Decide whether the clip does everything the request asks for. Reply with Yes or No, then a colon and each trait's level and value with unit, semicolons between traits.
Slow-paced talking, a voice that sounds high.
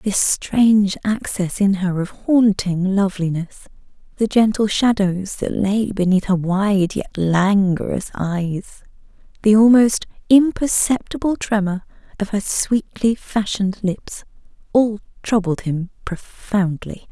Yes: slow, 110 wpm; high, 200 Hz